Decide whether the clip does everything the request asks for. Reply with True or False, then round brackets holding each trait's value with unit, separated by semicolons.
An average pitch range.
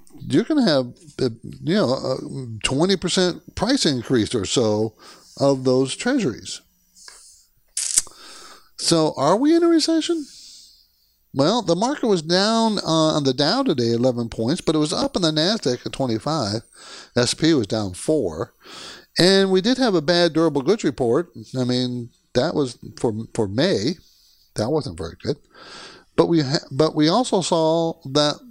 False (7.0 semitones)